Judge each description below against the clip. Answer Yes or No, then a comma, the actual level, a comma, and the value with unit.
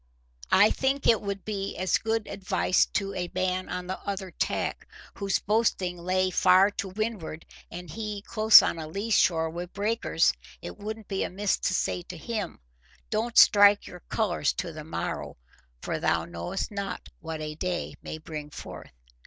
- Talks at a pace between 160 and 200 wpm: Yes, average, 170 wpm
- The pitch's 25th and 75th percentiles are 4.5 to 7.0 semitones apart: No, average, 3.4 semitones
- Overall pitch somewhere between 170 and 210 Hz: Yes, medium, 185 Hz